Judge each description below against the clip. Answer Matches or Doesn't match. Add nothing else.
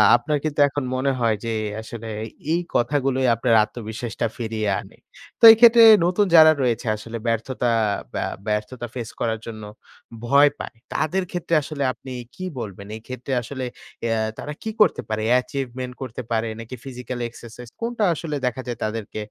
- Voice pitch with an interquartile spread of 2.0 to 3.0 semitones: Doesn't match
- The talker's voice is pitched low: Matches